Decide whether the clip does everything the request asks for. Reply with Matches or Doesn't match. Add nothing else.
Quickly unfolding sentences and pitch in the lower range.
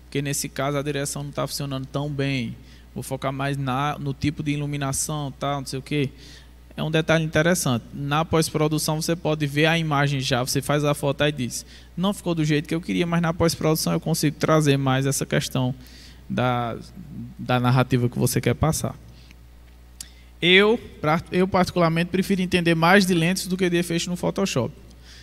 Doesn't match